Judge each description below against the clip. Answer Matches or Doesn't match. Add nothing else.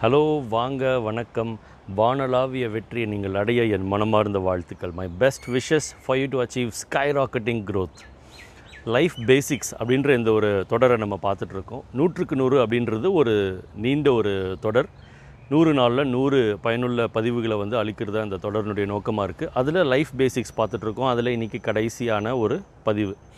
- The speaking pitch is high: Doesn't match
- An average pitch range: Matches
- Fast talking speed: Matches